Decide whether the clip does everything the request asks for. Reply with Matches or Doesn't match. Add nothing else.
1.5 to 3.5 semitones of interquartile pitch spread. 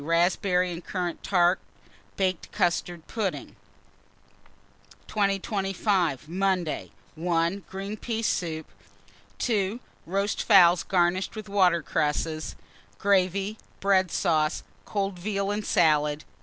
Matches